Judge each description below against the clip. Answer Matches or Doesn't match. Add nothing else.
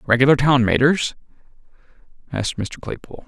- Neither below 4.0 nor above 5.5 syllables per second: Doesn't match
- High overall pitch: Doesn't match